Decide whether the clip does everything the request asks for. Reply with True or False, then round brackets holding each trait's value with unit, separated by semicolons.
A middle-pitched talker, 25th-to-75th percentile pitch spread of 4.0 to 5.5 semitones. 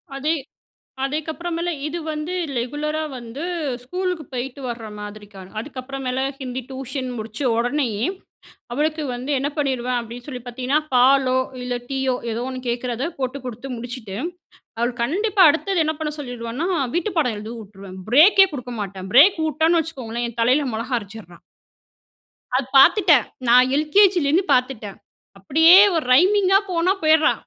False (265 Hz; 4.6 semitones)